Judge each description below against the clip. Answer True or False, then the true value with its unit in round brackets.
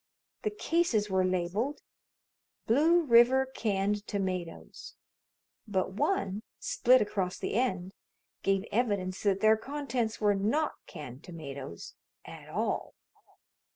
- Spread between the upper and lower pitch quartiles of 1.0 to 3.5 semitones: False (5.3 semitones)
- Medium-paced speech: False (110 wpm)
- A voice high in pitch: True (210 Hz)